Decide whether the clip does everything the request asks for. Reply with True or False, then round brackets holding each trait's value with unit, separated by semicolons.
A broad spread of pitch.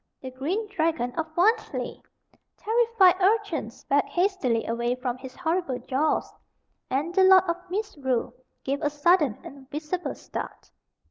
True (6.2 semitones)